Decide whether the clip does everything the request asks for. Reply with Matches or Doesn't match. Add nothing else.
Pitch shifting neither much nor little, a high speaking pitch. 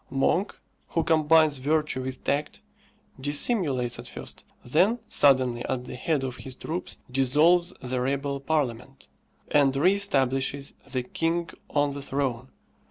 Doesn't match